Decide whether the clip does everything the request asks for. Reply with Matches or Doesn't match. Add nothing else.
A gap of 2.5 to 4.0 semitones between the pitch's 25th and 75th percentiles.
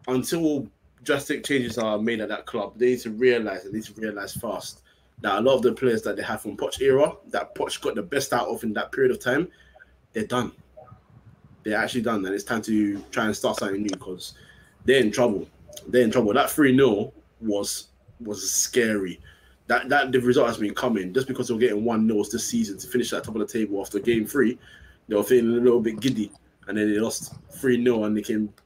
Matches